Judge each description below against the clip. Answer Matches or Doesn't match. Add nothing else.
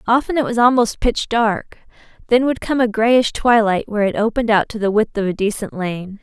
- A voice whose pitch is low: Doesn't match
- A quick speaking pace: Matches